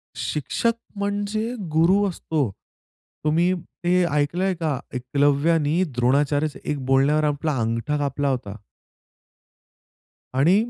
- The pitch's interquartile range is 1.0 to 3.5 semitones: No, average, 4.0 semitones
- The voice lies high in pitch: No, medium, 150 Hz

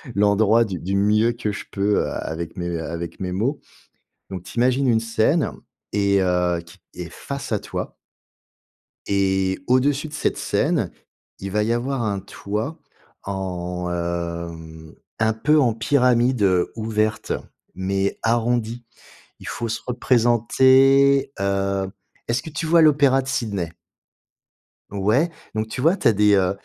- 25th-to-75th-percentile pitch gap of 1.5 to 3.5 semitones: No, average, 4.7 semitones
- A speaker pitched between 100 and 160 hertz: Yes, low, 105 Hz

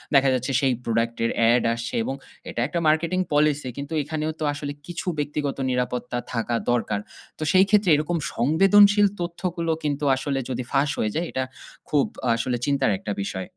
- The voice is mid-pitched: Yes, medium, 145 Hz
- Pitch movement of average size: Yes, average, 4.8 semitones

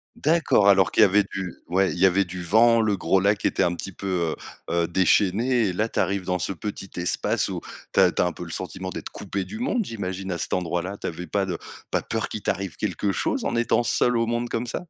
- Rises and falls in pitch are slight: No, average, 3.5 semitones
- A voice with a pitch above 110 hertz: No, very low, 95 Hz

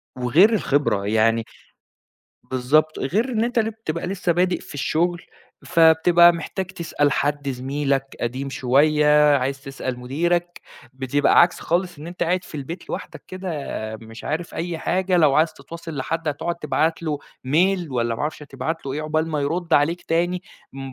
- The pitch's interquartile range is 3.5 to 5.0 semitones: Yes, average, 4.1 semitones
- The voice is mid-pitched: Yes, medium, 155 Hz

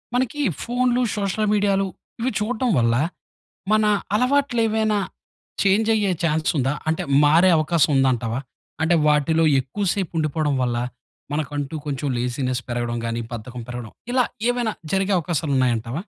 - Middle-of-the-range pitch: Yes, medium, 160 Hz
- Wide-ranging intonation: Yes, wide, 8.5 semitones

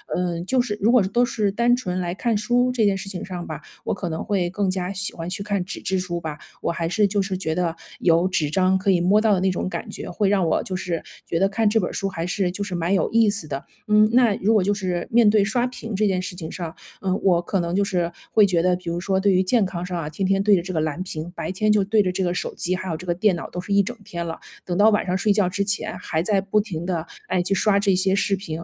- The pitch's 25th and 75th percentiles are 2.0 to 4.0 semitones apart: Yes, average, 2.7 semitones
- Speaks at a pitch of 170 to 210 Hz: Yes, high, 190 Hz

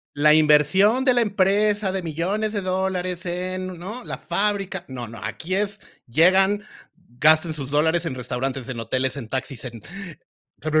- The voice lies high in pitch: No, medium, 175 Hz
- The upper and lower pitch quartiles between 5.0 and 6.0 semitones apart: Yes, wide, 5.5 semitones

